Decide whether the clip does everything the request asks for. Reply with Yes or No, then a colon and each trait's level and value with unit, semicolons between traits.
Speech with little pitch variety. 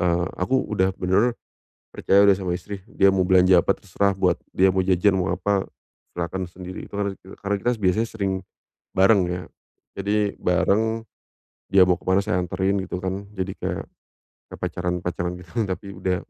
Yes: narrow, 1.8 semitones